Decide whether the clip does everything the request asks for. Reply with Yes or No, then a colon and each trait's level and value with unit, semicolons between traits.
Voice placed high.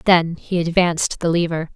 No: medium, 170 Hz